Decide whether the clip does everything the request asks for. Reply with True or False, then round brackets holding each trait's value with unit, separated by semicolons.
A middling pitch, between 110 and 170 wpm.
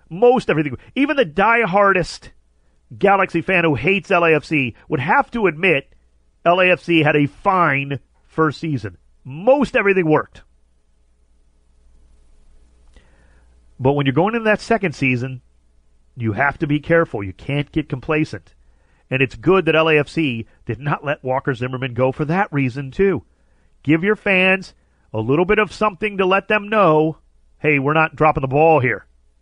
True (145 Hz; 150 wpm)